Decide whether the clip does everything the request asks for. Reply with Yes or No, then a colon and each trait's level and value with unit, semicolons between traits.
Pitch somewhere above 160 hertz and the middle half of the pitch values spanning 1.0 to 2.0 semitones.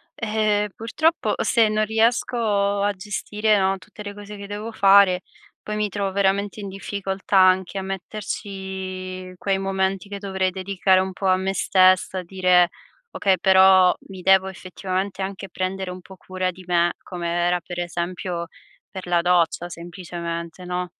Yes: high, 190 Hz; narrow, 1.6 semitones